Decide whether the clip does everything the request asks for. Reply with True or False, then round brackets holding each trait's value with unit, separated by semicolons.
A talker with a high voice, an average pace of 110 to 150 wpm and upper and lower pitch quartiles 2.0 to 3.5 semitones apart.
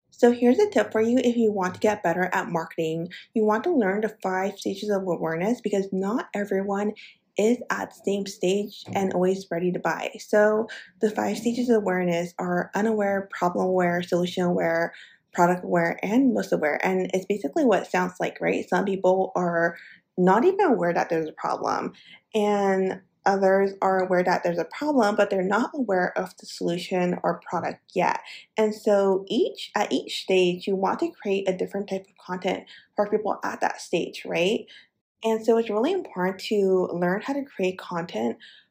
False (195 Hz; 190 wpm; 2.9 semitones)